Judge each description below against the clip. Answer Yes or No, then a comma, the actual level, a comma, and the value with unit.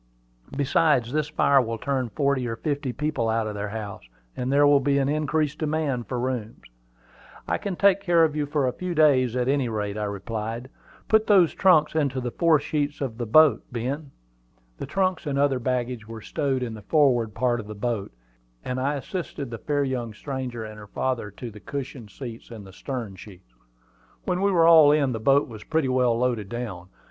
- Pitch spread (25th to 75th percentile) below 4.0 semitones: No, average, 4.5 semitones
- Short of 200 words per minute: No, fast, 205 wpm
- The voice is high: No, low, 130 Hz